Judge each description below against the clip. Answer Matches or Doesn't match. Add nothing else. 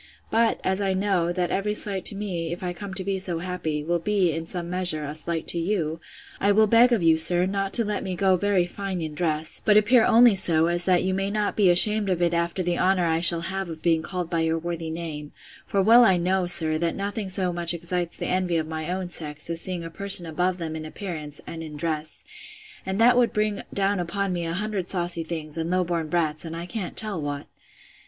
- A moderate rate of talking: Doesn't match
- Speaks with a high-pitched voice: Doesn't match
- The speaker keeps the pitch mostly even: Doesn't match